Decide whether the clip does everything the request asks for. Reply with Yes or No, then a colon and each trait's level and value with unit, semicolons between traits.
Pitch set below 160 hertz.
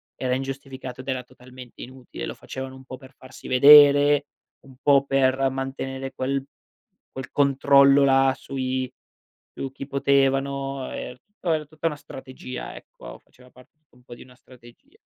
Yes: low, 135 Hz